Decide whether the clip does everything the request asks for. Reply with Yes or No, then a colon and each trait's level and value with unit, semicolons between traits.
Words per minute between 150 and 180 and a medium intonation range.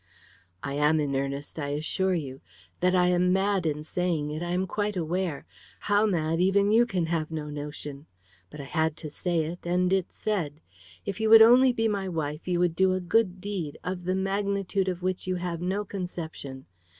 No: average, 200 wpm; average, 3.7 semitones